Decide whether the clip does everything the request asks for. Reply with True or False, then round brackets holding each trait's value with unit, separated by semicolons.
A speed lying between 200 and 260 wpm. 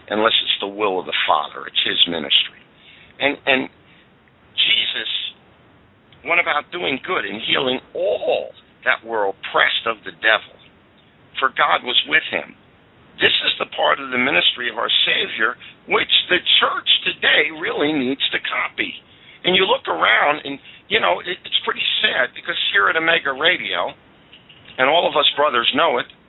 False (160 wpm)